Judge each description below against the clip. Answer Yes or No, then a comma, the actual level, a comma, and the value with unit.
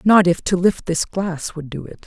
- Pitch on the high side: No, medium, 175 Hz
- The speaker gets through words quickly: Yes, fast, 260 wpm